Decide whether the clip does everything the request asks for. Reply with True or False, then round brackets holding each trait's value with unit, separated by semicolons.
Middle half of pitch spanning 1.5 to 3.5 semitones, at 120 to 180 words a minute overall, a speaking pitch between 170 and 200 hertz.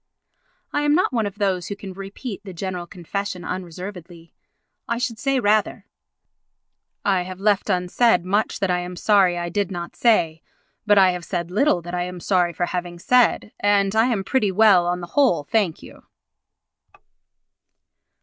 True (2.9 semitones; 170 wpm; 190 Hz)